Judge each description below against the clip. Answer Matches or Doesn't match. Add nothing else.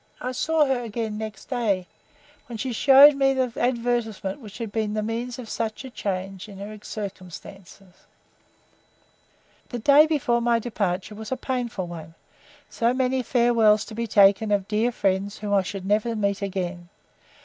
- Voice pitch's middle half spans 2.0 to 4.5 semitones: Matches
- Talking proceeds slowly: Doesn't match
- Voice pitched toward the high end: Matches